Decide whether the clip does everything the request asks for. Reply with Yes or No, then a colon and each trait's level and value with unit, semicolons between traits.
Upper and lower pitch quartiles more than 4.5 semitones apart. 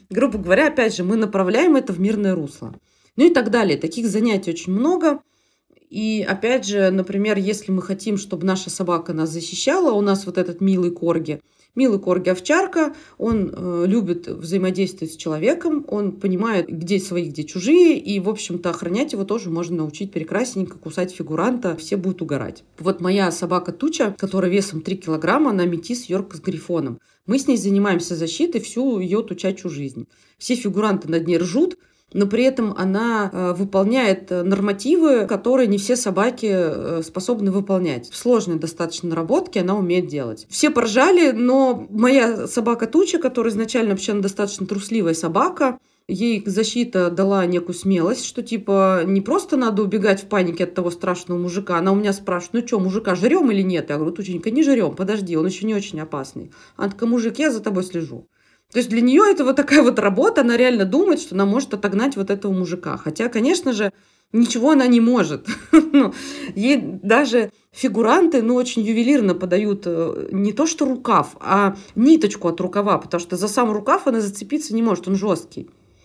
Yes: average, 5.1 semitones